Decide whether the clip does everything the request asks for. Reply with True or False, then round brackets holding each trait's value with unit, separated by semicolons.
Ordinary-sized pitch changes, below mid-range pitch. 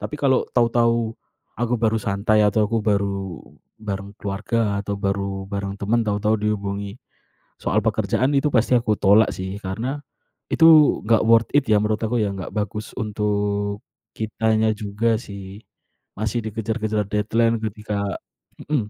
False (2.2 semitones; 110 Hz)